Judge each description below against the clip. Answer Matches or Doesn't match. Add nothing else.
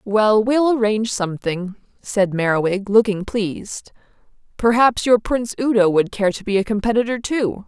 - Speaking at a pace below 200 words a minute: Matches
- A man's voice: Doesn't match